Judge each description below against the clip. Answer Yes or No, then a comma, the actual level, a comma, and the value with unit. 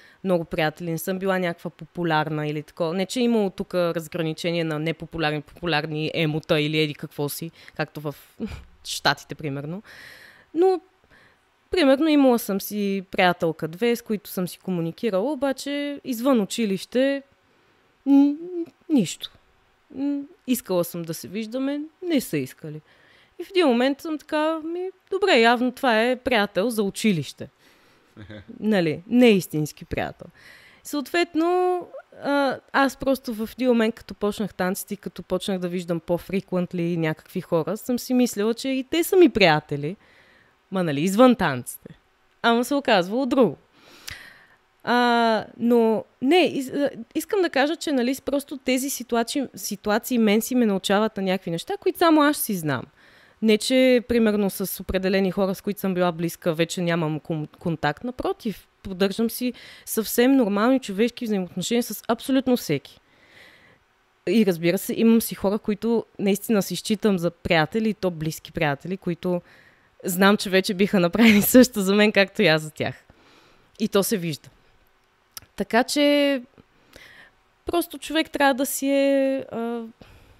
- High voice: Yes, high, 210 Hz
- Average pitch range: No, wide, 6.7 semitones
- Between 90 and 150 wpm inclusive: Yes, average, 145 wpm